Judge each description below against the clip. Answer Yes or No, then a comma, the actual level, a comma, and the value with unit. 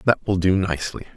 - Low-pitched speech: Yes, very low, 95 Hz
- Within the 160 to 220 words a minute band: Yes, fast, 205 wpm